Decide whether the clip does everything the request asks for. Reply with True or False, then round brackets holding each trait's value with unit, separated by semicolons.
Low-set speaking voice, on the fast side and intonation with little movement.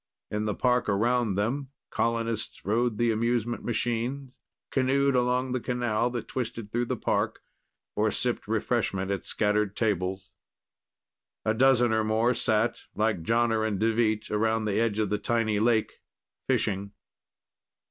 False (115 Hz; 140 wpm; 2.3 semitones)